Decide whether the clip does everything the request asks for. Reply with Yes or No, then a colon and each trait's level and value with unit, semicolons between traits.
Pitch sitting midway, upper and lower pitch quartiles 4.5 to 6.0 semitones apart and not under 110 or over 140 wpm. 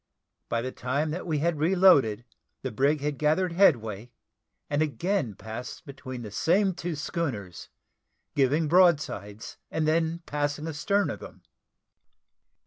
Yes: medium, 150 Hz; average, 5.1 semitones; slow, 135 wpm